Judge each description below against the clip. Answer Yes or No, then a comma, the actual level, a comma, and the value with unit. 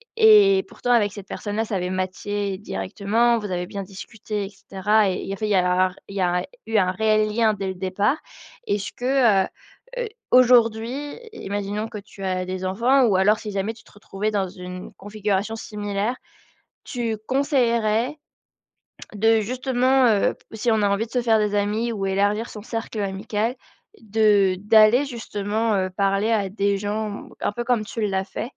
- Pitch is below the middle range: No, high, 210 Hz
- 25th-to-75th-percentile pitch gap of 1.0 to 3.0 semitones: Yes, narrow, 2.6 semitones